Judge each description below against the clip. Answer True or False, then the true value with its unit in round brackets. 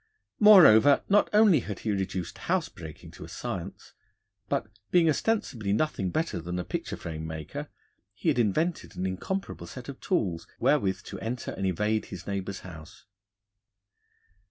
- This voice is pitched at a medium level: False (105 Hz)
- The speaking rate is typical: True (155 wpm)